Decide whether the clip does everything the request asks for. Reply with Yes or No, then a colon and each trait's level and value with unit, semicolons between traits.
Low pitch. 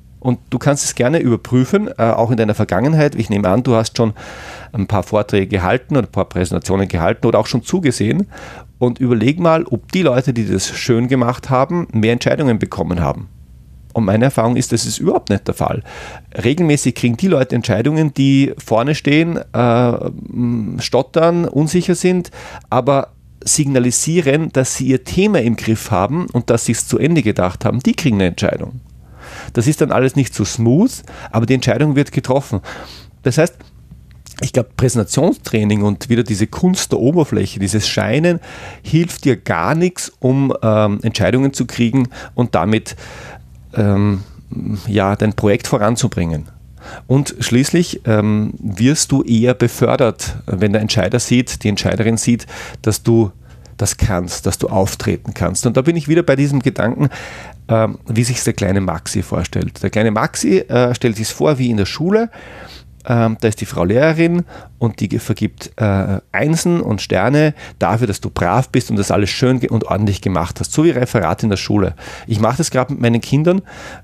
Yes: low, 120 Hz